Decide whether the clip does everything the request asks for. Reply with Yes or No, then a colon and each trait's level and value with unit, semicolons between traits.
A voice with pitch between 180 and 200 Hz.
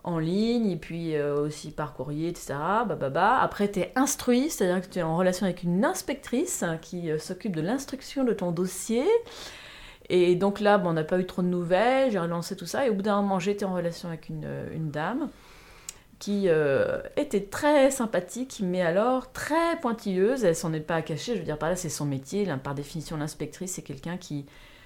Yes: medium, 185 Hz